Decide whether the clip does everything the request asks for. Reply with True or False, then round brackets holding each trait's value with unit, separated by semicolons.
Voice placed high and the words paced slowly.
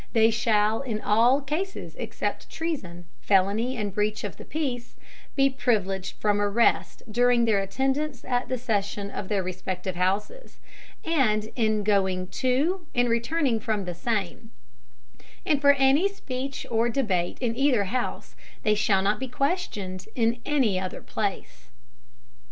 False (225 Hz; 145 wpm)